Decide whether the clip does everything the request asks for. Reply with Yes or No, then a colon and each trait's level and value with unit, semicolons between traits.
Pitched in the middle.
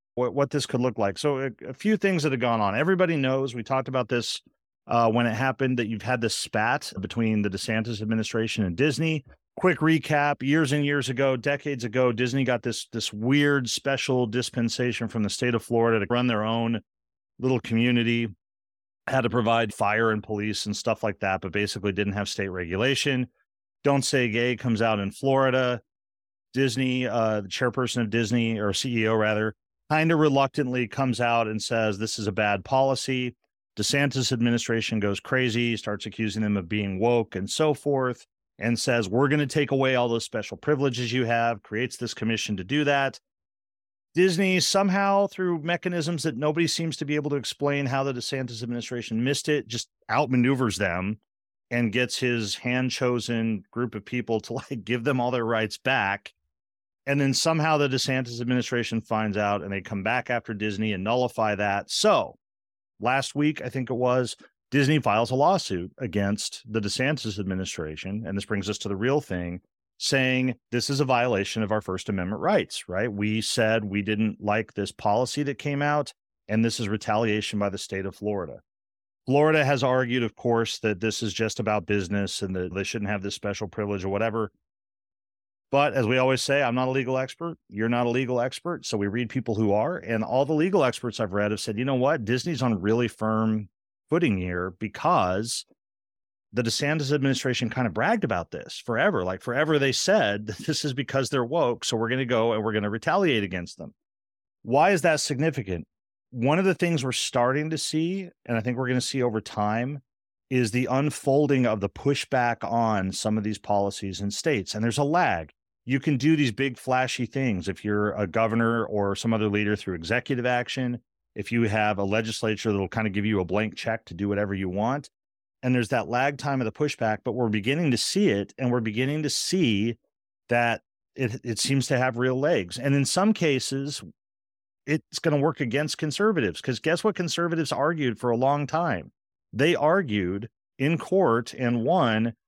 No: low, 120 Hz